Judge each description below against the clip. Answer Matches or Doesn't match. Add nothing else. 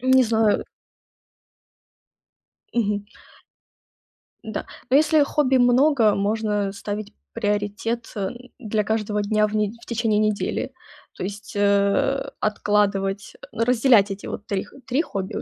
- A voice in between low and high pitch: Doesn't match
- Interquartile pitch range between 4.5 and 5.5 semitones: Doesn't match